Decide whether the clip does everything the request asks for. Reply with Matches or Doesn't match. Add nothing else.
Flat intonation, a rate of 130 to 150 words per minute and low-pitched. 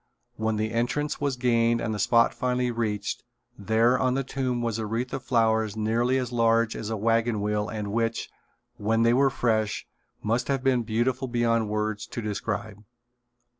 Doesn't match